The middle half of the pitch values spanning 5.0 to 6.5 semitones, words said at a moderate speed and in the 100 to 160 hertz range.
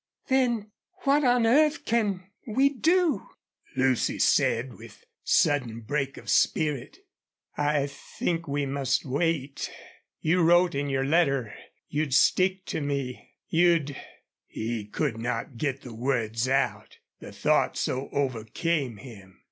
No: wide, 5.6 semitones; slow, 130 wpm; medium, 140 Hz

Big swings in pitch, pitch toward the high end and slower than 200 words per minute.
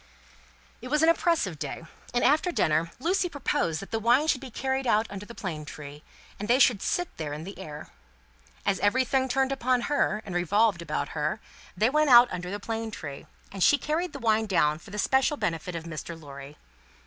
No: wide, 8.0 semitones; high, 215 Hz; fast, 205 wpm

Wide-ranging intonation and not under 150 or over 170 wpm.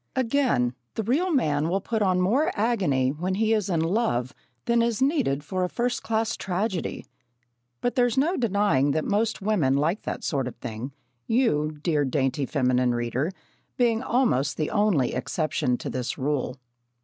Yes: wide, 8.7 semitones; average, 165 wpm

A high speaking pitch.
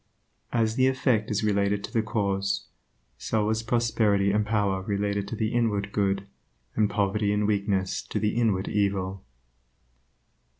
No: low, 105 Hz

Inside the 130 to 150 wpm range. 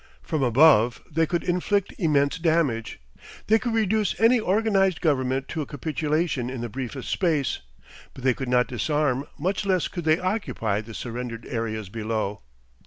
No: average, 160 wpm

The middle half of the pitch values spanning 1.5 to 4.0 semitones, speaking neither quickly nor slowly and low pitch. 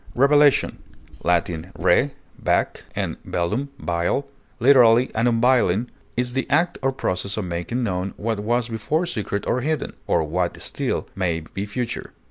No: average, 5.2 semitones; average, 145 wpm; low, 115 Hz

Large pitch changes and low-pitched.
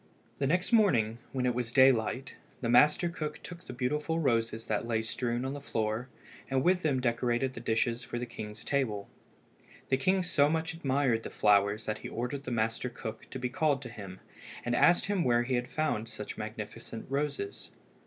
No: average, 4.0 semitones; low, 125 Hz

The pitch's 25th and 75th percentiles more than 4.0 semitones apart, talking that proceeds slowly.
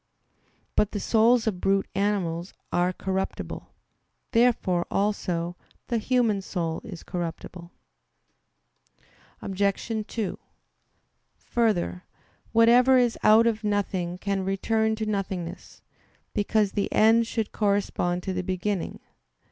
No: average, 3.3 semitones; slow, 110 wpm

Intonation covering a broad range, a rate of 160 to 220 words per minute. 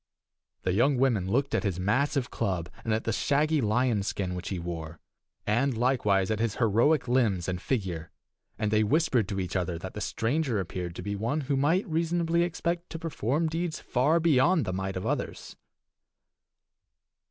Yes: wide, 7.3 semitones; average, 175 wpm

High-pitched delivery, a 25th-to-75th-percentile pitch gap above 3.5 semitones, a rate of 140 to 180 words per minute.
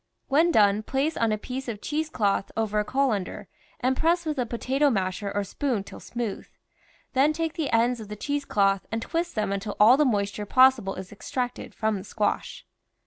No: high, 230 Hz; average, 5.0 semitones; fast, 205 wpm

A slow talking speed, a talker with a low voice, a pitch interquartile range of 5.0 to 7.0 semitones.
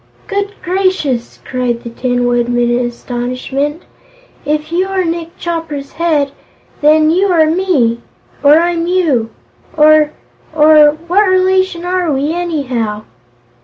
No: slow, 125 wpm; very high, 310 Hz; wide, 5.6 semitones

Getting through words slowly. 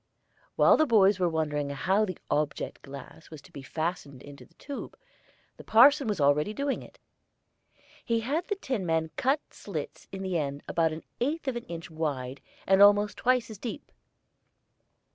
No: average, 170 wpm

